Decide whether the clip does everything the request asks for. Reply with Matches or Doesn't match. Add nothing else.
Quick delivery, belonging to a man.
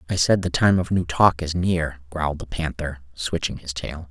Matches